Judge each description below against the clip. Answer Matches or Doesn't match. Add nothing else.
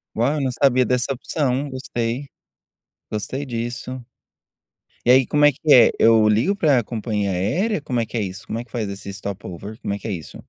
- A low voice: Matches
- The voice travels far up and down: Doesn't match